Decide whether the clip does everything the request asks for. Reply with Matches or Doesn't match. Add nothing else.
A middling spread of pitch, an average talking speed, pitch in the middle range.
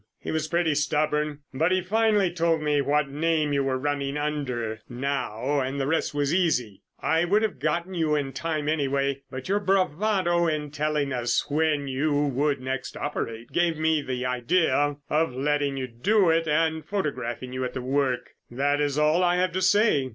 Matches